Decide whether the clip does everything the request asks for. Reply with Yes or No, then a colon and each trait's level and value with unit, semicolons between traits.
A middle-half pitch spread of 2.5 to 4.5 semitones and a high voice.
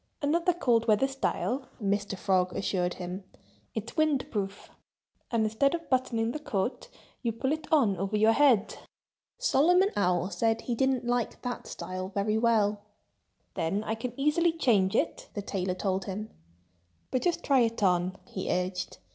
No: wide, 5.4 semitones; high, 225 Hz